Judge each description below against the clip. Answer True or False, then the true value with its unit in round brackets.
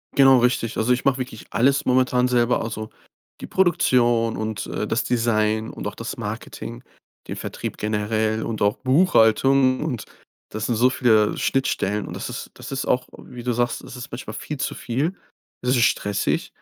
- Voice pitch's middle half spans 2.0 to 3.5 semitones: True (2.8 semitones)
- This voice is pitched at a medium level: False (120 Hz)